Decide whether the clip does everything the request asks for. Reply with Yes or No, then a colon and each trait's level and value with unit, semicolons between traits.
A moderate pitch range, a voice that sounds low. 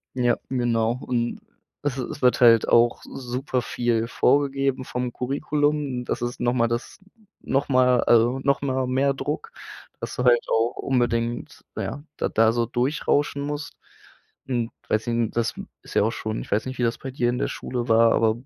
No: narrow, 2.3 semitones; low, 125 Hz